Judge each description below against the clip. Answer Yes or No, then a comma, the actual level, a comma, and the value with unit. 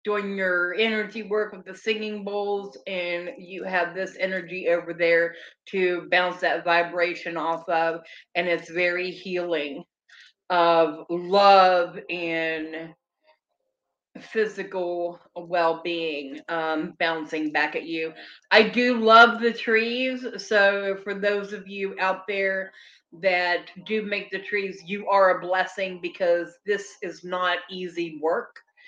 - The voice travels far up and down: No, average, 2.9 semitones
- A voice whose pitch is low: No, medium, 185 Hz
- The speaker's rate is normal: No, slow, 130 wpm